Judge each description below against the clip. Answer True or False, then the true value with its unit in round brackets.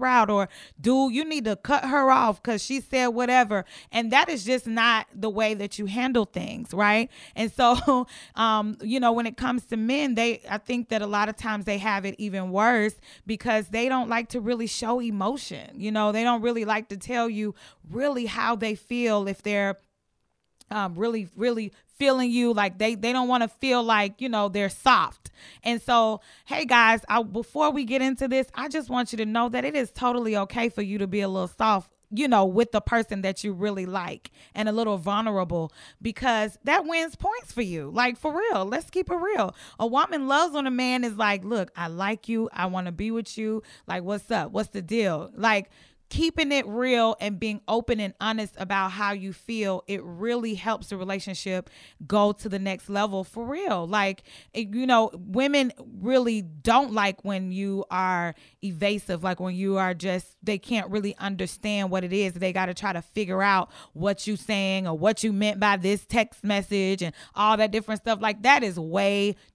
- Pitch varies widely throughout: False (3.3 semitones)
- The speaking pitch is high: True (215 Hz)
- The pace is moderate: False (210 wpm)